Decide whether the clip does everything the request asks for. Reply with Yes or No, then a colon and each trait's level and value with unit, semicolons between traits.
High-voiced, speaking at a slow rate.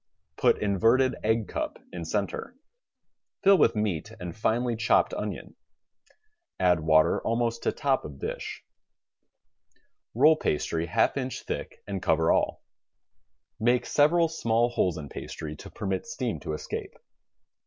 No: low, 110 Hz; slow, 130 wpm